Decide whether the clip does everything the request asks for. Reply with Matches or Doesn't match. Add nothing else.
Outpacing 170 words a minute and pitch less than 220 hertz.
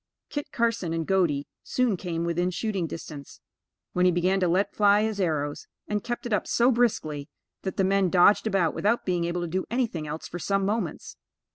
Matches